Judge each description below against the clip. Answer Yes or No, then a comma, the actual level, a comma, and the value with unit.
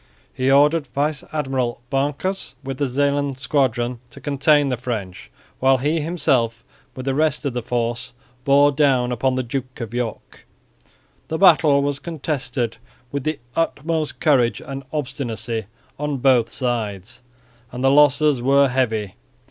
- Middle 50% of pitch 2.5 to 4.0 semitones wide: Yes, average, 2.9 semitones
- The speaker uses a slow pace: No, average, 145 wpm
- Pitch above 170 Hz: No, low, 135 Hz